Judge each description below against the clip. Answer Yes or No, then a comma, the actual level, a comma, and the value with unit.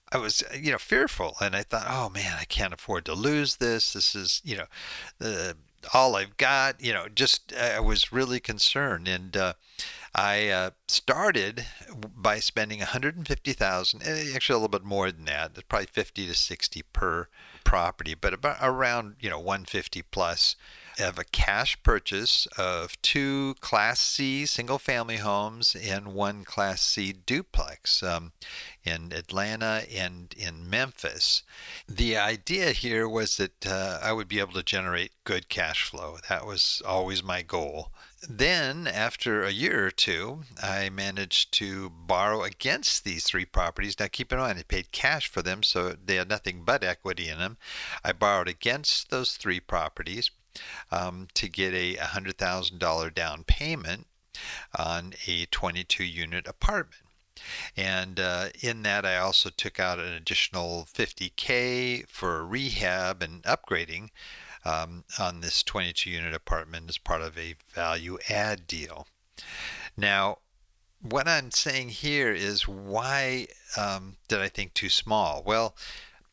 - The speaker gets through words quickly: No, average, 155 wpm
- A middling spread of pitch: Yes, average, 3.9 semitones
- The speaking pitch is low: Yes, low, 100 Hz